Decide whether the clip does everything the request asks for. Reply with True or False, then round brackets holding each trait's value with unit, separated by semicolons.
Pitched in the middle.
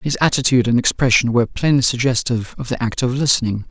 False (125 Hz)